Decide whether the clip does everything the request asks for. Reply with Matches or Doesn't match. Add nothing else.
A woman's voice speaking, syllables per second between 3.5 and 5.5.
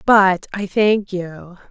Doesn't match